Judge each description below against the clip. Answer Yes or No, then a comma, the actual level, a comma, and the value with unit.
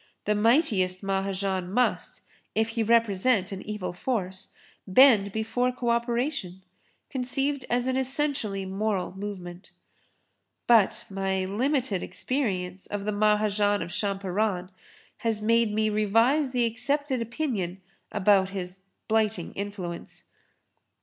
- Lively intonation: No, average, 3.9 semitones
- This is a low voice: No, high, 210 Hz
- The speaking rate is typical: No, slow, 115 wpm